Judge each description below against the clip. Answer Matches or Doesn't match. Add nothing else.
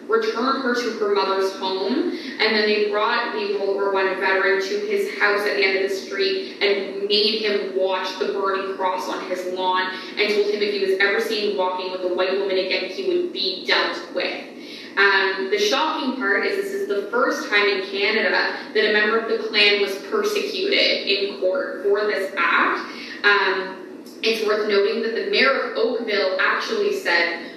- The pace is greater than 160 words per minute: Matches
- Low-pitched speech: Doesn't match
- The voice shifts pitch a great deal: Matches